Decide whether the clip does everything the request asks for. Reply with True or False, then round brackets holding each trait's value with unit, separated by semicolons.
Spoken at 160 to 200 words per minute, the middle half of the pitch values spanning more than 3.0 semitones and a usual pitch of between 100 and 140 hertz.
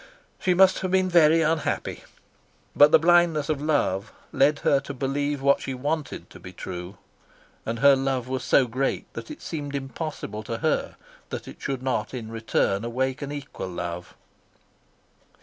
True (165 wpm; 4.4 semitones; 135 Hz)